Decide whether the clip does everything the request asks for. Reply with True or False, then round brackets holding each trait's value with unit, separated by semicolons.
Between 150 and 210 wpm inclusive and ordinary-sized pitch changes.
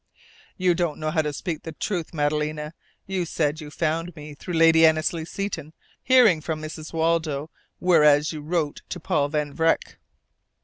False (165 wpm; 1.9 semitones)